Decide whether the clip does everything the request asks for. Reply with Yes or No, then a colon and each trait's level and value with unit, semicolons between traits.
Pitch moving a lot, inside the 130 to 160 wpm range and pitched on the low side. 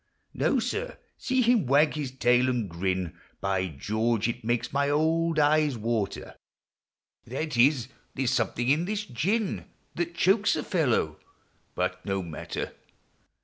Yes: wide, 7.0 semitones; average, 150 wpm; low, 130 Hz